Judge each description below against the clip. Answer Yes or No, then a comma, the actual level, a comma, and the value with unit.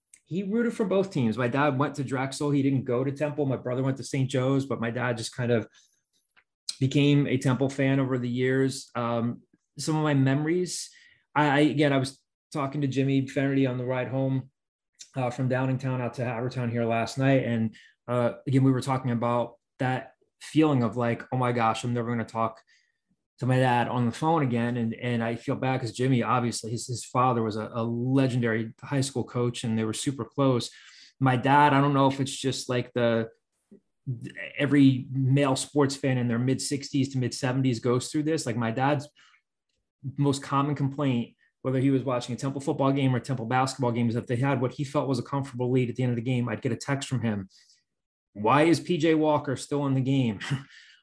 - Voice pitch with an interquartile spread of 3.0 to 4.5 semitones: No, narrow, 2.4 semitones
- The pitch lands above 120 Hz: Yes, low, 130 Hz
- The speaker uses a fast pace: Yes, fast, 215 wpm